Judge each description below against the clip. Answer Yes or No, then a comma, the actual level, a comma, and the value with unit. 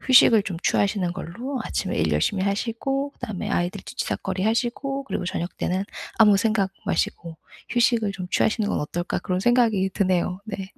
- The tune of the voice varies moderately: Yes, average, 4.2 semitones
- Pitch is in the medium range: No, high, 200 Hz